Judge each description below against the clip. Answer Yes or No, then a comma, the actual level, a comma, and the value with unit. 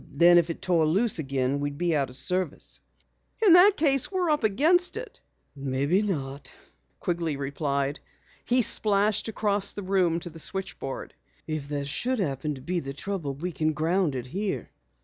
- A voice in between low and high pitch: Yes, medium, 170 Hz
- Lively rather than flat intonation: Yes, wide, 6.3 semitones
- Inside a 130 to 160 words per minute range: No, average, 170 wpm